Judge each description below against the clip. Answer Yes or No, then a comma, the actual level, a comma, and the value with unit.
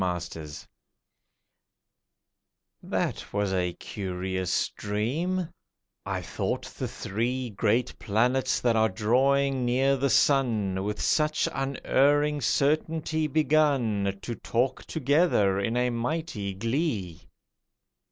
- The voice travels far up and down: Yes, wide, 5.7 semitones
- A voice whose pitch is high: No, low, 125 Hz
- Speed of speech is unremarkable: No, slow, 105 wpm